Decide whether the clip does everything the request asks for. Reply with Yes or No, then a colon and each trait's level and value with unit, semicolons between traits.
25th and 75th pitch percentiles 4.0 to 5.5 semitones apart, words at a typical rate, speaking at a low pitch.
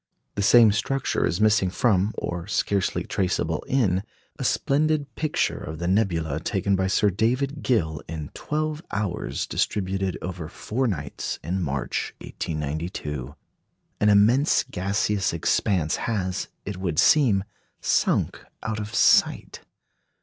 No: average, 4.5 semitones; slow, 130 wpm; very low, 95 Hz